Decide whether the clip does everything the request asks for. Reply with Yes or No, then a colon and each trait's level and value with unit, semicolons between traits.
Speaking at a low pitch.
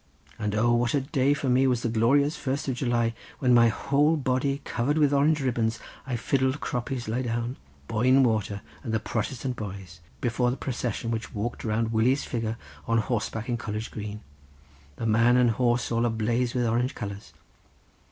Yes: low, 120 Hz